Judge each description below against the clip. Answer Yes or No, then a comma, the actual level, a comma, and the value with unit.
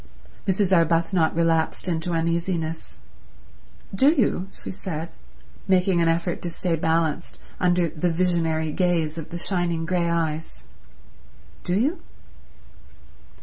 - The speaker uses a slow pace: Yes, slow, 115 wpm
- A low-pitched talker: No, medium, 170 Hz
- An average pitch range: No, narrow, 1.8 semitones